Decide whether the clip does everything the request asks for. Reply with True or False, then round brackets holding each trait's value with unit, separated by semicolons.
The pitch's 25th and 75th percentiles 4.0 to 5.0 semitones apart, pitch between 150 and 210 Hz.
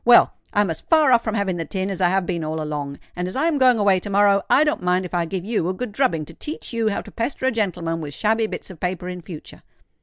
True (4.6 semitones; 190 Hz)